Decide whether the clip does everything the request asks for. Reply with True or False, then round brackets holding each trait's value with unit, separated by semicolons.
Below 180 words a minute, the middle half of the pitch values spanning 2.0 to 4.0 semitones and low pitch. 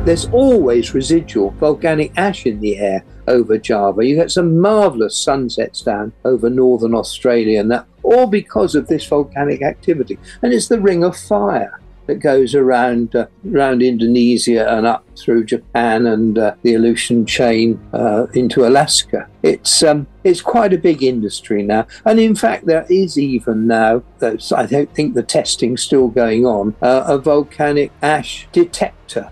False (160 wpm; 5.4 semitones; 125 Hz)